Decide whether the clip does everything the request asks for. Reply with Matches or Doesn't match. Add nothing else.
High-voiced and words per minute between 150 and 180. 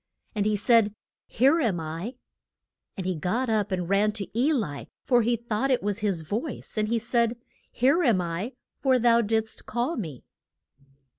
Matches